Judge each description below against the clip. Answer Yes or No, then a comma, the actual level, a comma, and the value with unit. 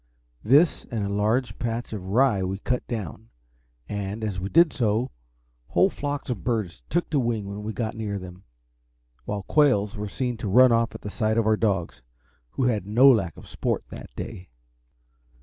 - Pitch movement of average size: Yes, average, 3.4 semitones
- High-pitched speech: No, low, 110 Hz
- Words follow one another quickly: No, average, 185 wpm